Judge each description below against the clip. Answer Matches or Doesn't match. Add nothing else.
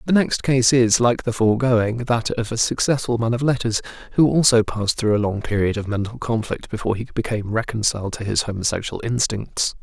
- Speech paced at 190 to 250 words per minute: Matches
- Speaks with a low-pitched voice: Matches